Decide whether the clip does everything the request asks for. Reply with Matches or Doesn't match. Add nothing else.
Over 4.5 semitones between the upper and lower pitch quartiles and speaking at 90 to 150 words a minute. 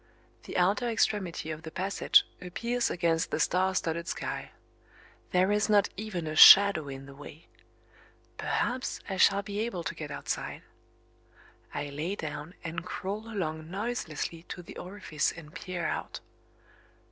Doesn't match